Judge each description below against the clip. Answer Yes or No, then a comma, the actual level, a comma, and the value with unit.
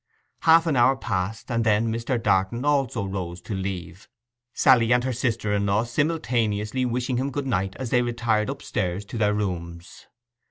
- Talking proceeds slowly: No, average, 170 wpm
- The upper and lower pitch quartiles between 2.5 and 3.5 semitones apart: No, average, 4.0 semitones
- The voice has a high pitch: No, low, 115 Hz